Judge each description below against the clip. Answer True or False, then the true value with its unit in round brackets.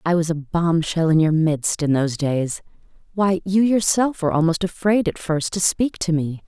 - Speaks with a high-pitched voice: False (170 Hz)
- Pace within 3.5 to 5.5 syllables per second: True (4.8 syllables/s)